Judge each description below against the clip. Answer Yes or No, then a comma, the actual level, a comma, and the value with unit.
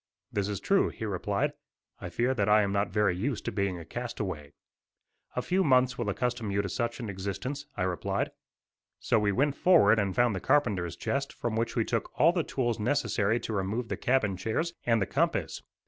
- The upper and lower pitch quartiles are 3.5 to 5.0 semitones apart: Yes, average, 4.2 semitones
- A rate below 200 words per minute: No, fast, 205 wpm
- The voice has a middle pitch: No, low, 110 Hz